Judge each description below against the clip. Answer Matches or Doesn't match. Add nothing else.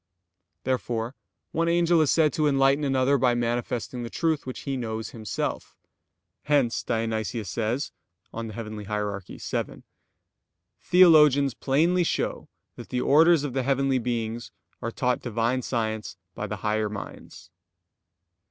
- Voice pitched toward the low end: Matches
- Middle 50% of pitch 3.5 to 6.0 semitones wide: Matches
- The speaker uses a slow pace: Matches